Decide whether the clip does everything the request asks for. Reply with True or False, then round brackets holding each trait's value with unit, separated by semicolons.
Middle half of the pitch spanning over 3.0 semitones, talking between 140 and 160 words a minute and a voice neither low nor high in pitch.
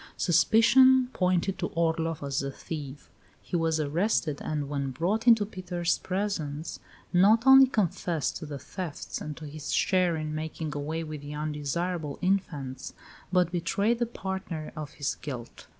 True (4.3 semitones; 150 wpm; 165 Hz)